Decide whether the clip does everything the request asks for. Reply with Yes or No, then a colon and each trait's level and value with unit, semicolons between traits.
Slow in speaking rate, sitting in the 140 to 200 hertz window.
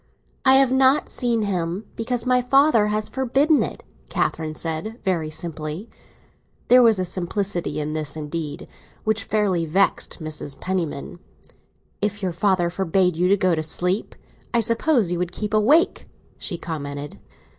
No: average, 150 wpm; high, 190 Hz